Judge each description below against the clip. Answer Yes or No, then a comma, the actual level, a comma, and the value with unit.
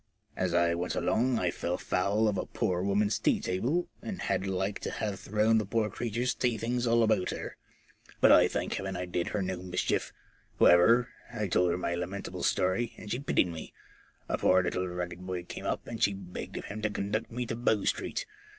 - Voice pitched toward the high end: No, low, 100 Hz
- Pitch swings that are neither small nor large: Yes, average, 3.7 semitones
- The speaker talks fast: Yes, fast, 210 wpm